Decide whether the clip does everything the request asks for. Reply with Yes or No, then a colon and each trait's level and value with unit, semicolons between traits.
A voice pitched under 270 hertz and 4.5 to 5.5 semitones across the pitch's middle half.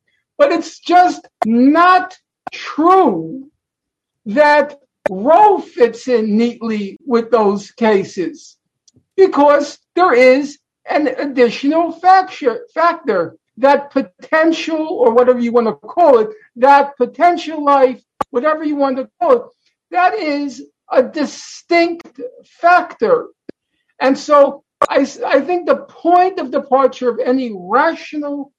No: very high, 285 Hz; average, 5.1 semitones